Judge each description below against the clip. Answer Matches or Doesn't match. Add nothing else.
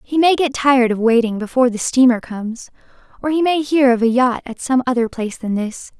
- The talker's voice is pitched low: Doesn't match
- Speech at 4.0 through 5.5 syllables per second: Doesn't match